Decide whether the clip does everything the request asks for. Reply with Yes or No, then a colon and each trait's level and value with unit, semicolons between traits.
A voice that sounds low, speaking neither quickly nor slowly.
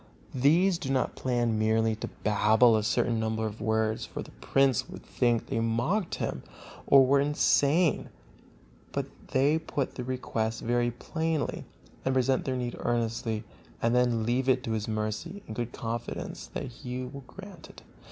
Yes: low, 120 Hz; average, 165 wpm